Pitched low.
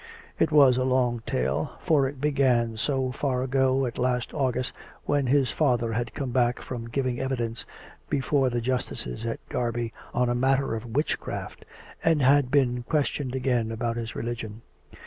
Yes: low, 125 Hz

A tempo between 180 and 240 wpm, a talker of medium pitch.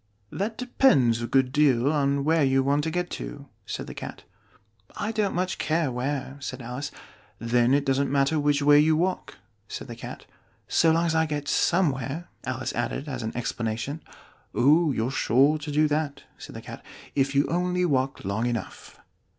Yes: average, 190 wpm; medium, 145 Hz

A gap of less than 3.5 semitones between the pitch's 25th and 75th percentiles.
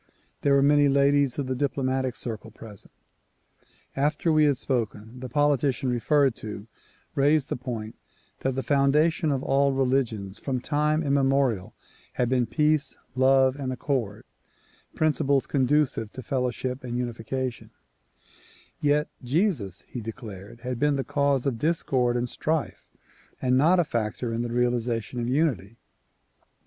Yes: average, 3.0 semitones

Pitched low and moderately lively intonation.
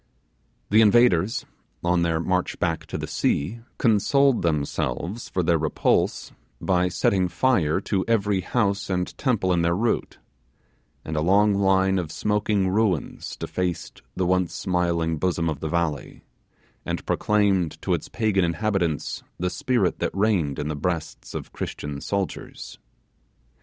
Yes: very low, 90 Hz; average, 3.6 semitones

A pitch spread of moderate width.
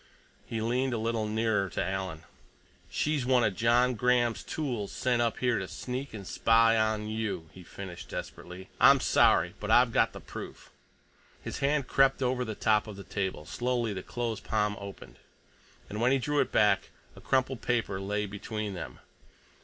Yes: average, 3.6 semitones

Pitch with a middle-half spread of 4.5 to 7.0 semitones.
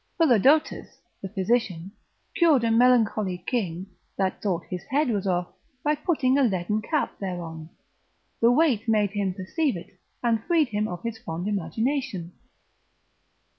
Yes: wide, 5.5 semitones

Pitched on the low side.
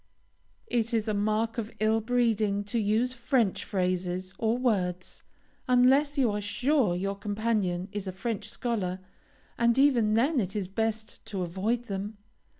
No: high, 215 Hz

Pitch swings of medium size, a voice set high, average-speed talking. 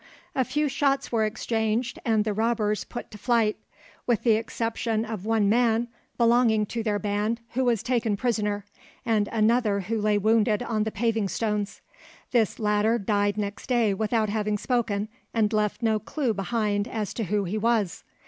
No: narrow, 1.9 semitones; high, 220 Hz; average, 170 wpm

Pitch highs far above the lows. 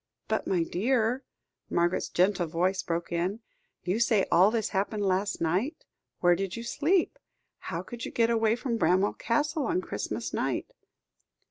No: average, 4.6 semitones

